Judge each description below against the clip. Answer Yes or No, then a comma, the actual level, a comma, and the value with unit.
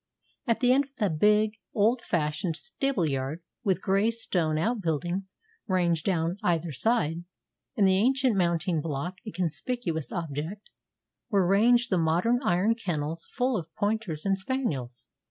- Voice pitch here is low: No, medium, 185 Hz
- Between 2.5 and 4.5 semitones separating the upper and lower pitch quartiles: No, wide, 5.5 semitones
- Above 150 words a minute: No, average, 145 wpm